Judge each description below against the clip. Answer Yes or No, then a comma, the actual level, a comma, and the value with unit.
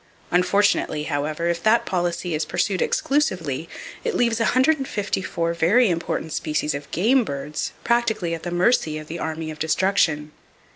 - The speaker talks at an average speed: Yes, average, 145 wpm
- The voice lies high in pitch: No, medium, 170 Hz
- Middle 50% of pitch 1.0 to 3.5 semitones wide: No, wide, 5.6 semitones